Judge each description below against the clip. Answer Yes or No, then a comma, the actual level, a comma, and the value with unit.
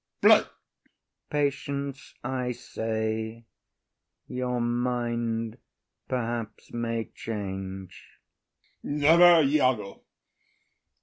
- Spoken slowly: Yes, slow, 65 wpm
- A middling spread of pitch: Yes, average, 3.0 semitones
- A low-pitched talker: Yes, low, 120 Hz